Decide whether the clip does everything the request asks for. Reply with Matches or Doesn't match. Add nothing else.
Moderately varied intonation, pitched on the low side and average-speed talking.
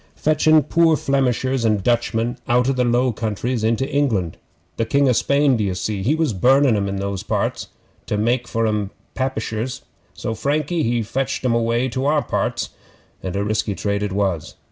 Matches